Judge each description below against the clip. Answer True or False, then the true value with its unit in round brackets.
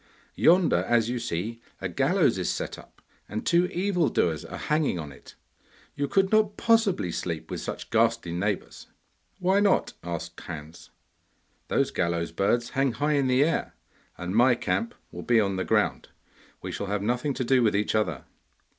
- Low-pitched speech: True (120 Hz)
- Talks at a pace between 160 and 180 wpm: True (175 wpm)